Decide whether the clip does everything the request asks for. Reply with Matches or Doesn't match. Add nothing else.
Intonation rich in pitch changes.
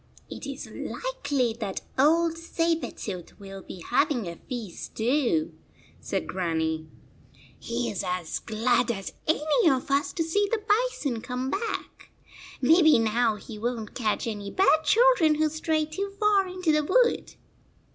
Matches